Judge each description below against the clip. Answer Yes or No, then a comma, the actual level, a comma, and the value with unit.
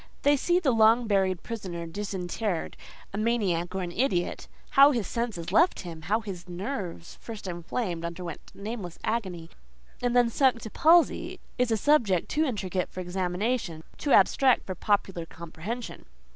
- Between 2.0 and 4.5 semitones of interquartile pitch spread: No, average, 5.3 semitones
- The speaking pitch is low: No, high, 200 Hz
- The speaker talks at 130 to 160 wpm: Yes, average, 145 wpm